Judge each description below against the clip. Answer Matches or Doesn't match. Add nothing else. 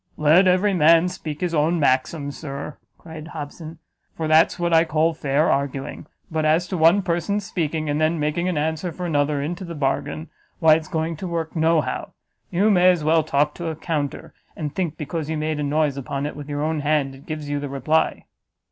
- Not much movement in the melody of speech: Matches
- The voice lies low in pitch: Doesn't match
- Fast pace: Matches